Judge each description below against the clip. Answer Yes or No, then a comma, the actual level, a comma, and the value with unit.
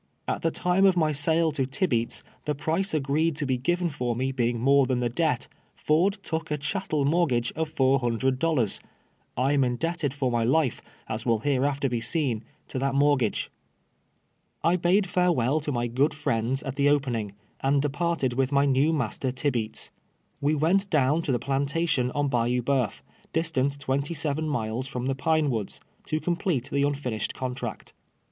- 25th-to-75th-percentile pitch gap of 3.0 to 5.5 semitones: Yes, average, 3.9 semitones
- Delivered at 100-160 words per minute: No, average, 180 wpm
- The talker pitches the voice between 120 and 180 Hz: Yes, medium, 140 Hz